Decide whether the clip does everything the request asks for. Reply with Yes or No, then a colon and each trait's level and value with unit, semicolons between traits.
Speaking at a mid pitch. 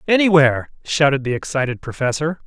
Yes: medium, 145 Hz